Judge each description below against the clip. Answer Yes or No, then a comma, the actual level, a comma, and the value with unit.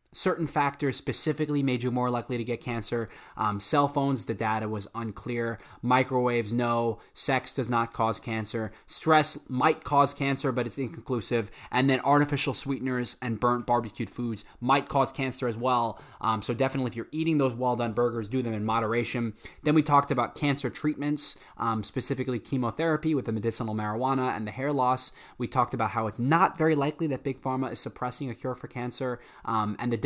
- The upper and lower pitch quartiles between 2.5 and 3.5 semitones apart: Yes, average, 3.0 semitones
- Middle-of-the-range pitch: No, low, 125 Hz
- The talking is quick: No, average, 190 wpm